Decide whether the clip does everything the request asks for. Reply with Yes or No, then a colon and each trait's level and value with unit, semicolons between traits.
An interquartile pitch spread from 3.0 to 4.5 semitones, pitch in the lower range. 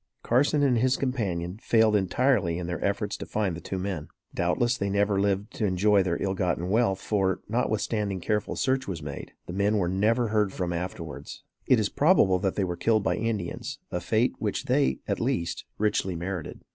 Yes: average, 3.4 semitones; low, 100 Hz